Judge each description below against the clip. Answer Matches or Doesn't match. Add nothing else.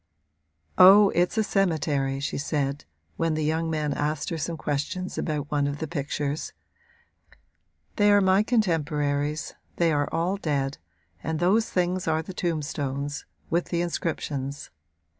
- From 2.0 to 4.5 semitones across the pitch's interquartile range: Matches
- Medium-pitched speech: Matches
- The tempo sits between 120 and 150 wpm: Matches